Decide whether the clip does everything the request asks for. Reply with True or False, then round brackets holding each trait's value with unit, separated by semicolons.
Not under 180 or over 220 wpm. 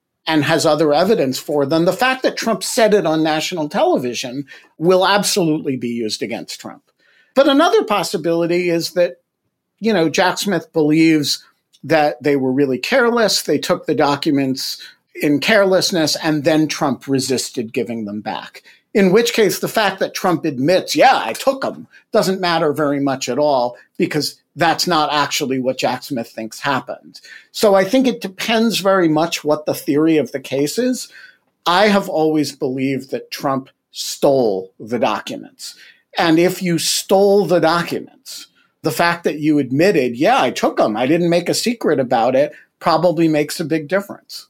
False (170 wpm)